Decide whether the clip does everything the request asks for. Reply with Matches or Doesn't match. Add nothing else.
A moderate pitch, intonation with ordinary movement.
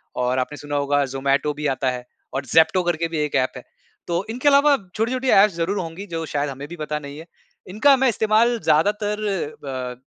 Doesn't match